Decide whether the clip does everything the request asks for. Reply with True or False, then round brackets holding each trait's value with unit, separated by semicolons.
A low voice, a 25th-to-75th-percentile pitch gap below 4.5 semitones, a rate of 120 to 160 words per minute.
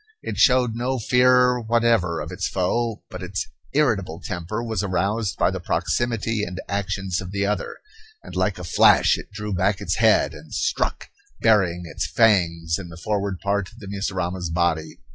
False (100 Hz; 4.0 semitones; 175 wpm)